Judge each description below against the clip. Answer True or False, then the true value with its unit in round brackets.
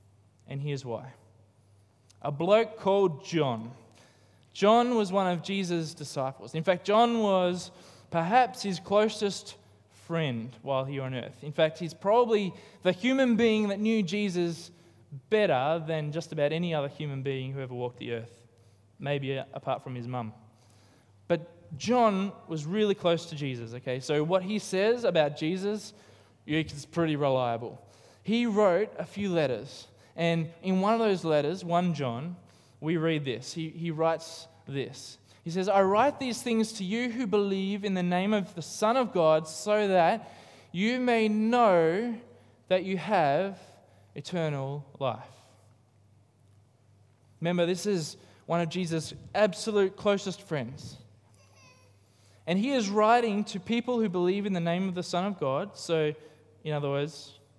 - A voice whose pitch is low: False (160 Hz)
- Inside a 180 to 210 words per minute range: False (155 wpm)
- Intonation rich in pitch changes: True (7.6 semitones)